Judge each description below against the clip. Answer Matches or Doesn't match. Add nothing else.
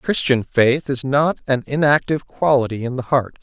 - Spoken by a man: Matches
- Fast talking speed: Doesn't match